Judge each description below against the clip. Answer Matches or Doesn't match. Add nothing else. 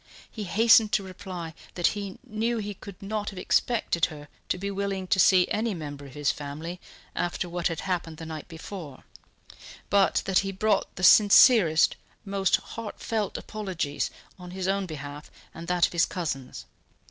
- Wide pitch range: Doesn't match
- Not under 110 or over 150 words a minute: Doesn't match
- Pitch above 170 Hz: Matches